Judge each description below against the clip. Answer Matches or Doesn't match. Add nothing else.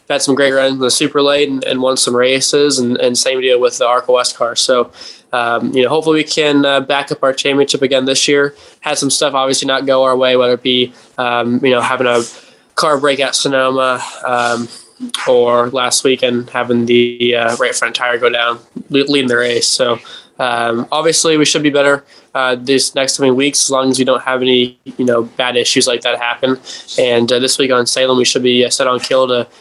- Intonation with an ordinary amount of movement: Doesn't match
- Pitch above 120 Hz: Matches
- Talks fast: Matches